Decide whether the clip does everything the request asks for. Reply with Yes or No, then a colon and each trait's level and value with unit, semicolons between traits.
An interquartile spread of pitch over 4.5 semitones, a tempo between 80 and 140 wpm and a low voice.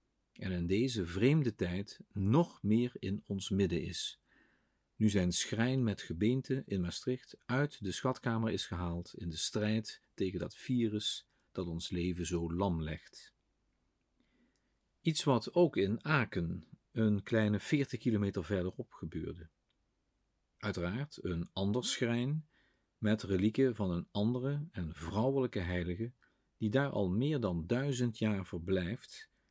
Yes: wide, 5.6 semitones; slow, 135 wpm; low, 105 Hz